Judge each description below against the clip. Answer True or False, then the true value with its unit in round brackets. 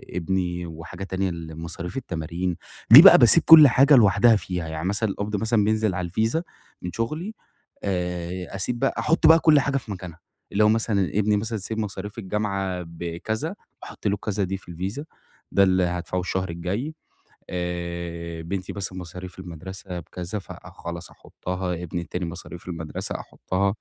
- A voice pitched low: True (95 Hz)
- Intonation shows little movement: False (3.4 semitones)